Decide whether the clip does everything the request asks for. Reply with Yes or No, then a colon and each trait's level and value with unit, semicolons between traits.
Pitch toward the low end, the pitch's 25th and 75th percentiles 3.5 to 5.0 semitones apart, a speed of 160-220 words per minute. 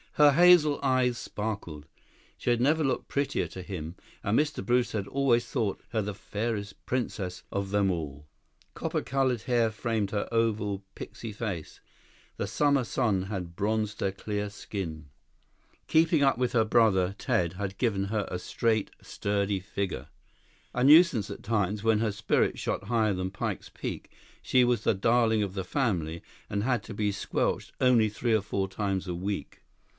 Yes: low, 105 Hz; average, 3.8 semitones; average, 170 wpm